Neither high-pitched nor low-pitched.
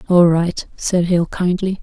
Yes: medium, 175 Hz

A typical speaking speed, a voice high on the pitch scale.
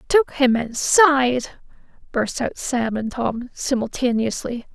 No: slow, 115 wpm; very high, 255 Hz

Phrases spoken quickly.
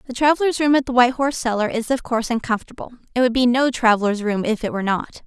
Yes: fast, 250 wpm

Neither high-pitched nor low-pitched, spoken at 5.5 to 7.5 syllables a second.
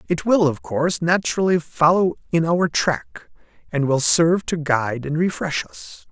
No: medium, 150 Hz; 4.7 syllables/s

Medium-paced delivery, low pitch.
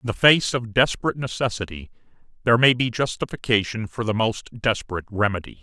Yes: average, 160 wpm; low, 115 Hz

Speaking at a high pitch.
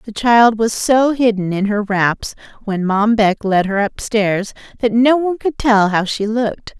Yes: high, 220 Hz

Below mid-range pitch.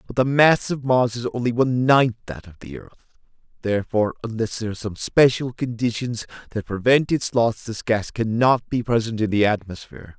Yes: low, 115 Hz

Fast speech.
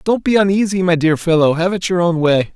Yes: fast, 260 wpm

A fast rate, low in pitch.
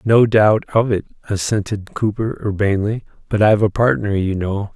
No: average, 165 wpm; low, 105 Hz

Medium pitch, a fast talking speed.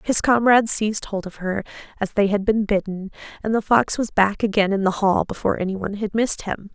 No: high, 205 Hz; fast, 220 wpm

